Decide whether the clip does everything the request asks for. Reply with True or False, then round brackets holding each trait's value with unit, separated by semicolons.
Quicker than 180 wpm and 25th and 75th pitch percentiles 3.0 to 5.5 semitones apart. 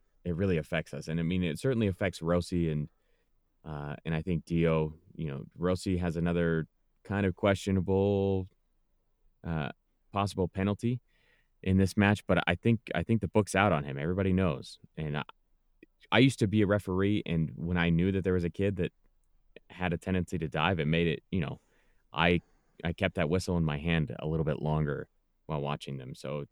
True (195 wpm; 3.3 semitones)